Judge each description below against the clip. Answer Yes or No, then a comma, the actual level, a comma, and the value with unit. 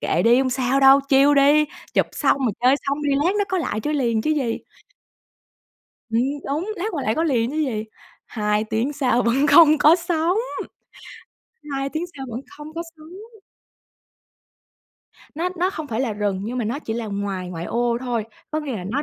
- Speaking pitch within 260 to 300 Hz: Yes, very high, 270 Hz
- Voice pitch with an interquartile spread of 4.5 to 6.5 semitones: Yes, average, 5.0 semitones